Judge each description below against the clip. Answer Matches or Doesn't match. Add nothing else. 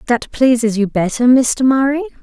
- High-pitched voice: Matches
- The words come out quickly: Doesn't match